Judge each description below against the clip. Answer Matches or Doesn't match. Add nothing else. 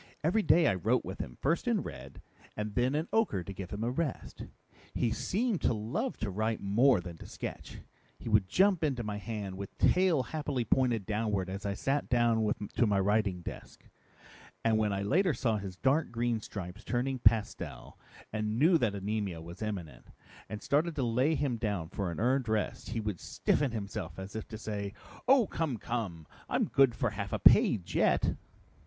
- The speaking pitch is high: Doesn't match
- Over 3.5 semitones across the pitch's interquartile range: Matches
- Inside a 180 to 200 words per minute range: Matches